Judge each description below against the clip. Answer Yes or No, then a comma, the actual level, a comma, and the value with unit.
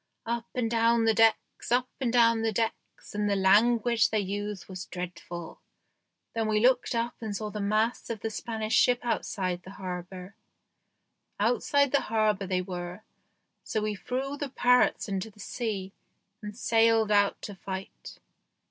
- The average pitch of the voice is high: Yes, high, 215 Hz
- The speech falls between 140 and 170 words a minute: Yes, average, 160 wpm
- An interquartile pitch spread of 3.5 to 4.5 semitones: No, average, 3.0 semitones